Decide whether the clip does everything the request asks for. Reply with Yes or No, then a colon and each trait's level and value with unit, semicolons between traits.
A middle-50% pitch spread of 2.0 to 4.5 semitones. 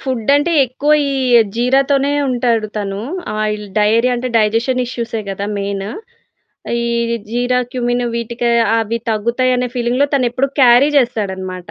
Yes: average, 2.9 semitones